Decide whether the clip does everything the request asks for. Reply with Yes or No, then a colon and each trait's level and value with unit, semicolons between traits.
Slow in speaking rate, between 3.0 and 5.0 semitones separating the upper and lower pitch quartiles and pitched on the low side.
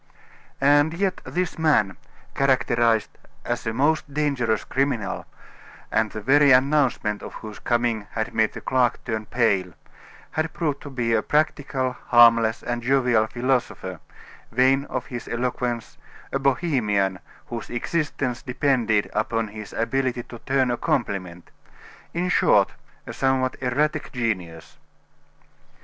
Yes: slow, 130 wpm; average, 3.5 semitones; low, 125 Hz